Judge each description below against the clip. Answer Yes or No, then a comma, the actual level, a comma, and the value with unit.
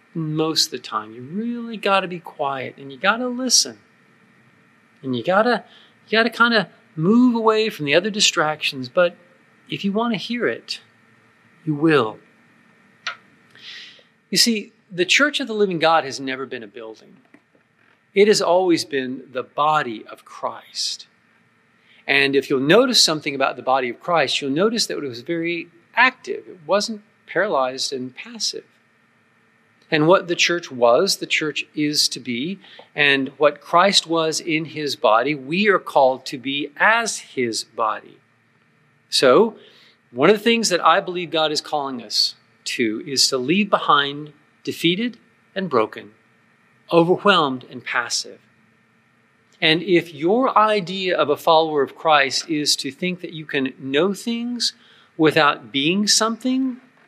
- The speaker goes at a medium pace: Yes, average, 160 wpm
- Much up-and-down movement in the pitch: Yes, wide, 6.7 semitones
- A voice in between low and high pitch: Yes, medium, 170 Hz